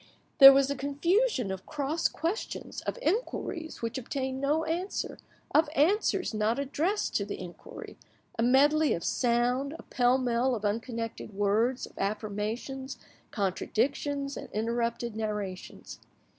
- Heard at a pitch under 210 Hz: No, very high, 260 Hz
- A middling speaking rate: No, slow, 130 wpm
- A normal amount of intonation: Yes, average, 4.2 semitones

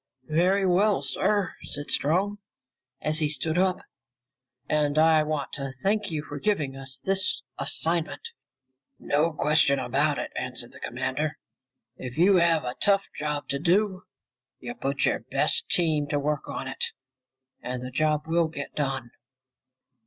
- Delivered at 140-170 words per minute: Yes, average, 150 wpm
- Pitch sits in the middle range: Yes, medium, 155 Hz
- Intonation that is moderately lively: Yes, average, 4.0 semitones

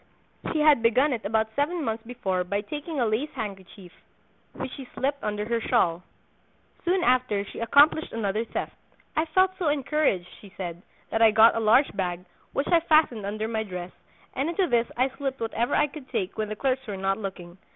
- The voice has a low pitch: No, high, 230 Hz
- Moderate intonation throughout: No, wide, 5.7 semitones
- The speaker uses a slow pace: No, average, 195 wpm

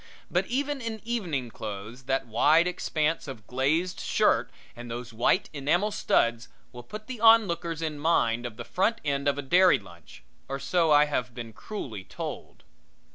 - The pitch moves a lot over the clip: Yes, wide, 7.0 semitones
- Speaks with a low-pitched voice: No, medium, 145 Hz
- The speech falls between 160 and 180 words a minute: Yes, average, 170 wpm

